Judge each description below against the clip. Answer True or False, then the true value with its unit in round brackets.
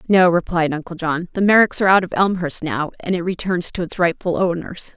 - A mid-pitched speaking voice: True (175 Hz)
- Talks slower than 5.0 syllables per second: False (5.7 syllables/s)